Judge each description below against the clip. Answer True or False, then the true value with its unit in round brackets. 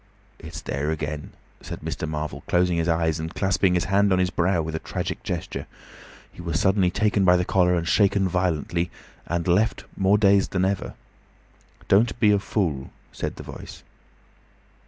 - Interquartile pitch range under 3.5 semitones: True (3.1 semitones)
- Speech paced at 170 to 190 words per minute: True (175 wpm)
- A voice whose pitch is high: False (90 Hz)